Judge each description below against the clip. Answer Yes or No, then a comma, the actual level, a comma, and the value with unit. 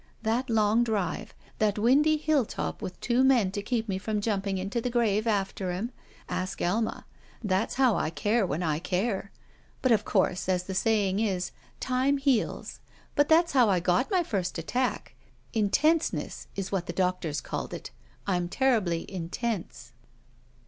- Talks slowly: No, average, 160 wpm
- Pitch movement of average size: Yes, average, 4.5 semitones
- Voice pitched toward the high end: Yes, high, 210 Hz